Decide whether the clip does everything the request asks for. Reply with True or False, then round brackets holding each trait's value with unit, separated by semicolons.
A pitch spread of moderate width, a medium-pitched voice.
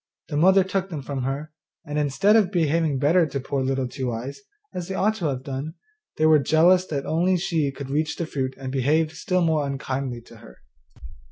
True (4.0 semitones; 150 Hz)